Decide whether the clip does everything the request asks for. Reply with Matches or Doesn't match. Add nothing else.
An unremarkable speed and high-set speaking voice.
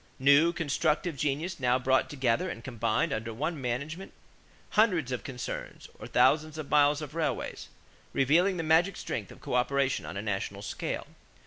Doesn't match